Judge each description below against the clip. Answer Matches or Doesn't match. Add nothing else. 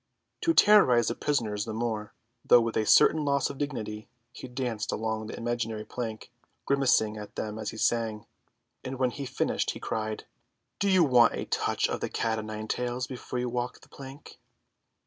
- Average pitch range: Matches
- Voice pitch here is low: Matches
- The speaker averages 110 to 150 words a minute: Doesn't match